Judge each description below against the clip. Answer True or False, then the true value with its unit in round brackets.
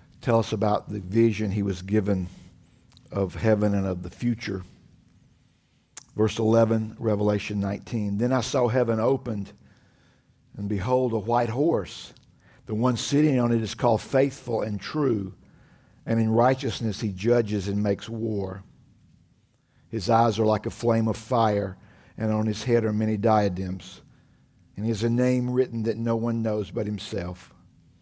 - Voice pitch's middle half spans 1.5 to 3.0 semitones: True (2.6 semitones)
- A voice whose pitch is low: True (110 Hz)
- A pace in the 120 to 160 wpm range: True (155 wpm)